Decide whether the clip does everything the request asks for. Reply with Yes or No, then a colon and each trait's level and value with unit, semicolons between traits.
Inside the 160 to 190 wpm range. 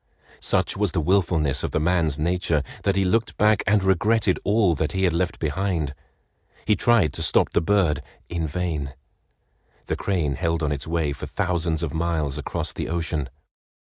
Yes: average, 175 wpm